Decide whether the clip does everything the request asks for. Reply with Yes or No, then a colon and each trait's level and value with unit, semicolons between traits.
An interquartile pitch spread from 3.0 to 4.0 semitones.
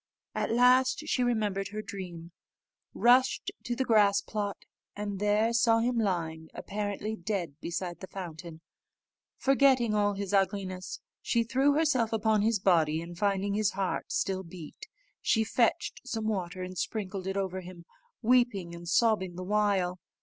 Yes: average, 3.6 semitones